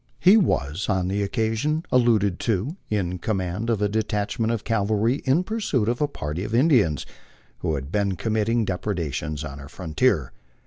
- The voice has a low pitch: Yes, low, 105 Hz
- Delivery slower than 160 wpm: No, average, 170 wpm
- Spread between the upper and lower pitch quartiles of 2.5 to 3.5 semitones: No, average, 4.7 semitones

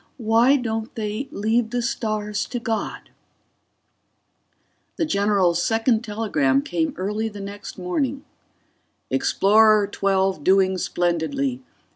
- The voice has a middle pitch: No, high, 215 Hz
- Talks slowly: Yes, slow, 105 wpm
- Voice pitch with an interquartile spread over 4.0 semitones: No, average, 3.1 semitones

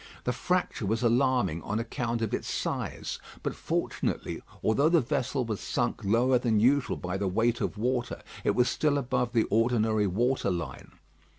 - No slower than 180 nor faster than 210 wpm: No, average, 170 wpm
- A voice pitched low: Yes, low, 120 Hz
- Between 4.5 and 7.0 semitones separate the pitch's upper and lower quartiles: No, average, 2.7 semitones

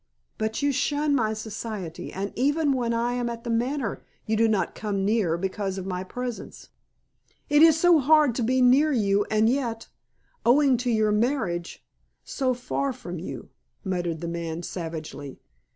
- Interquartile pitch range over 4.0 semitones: Yes, average, 5.1 semitones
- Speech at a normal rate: Yes, average, 170 wpm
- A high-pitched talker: Yes, high, 230 Hz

